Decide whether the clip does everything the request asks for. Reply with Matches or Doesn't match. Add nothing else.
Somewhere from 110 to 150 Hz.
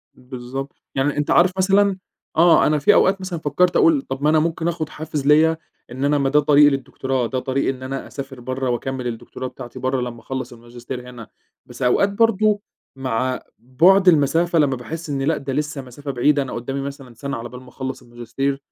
Matches